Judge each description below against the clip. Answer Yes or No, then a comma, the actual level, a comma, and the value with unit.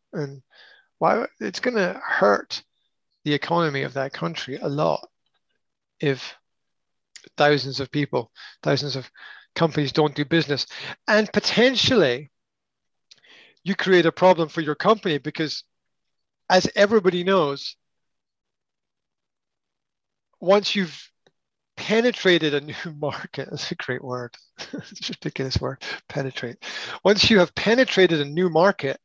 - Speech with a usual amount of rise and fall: Yes, average, 4.7 semitones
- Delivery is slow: Yes, slow, 115 wpm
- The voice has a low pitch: No, medium, 160 Hz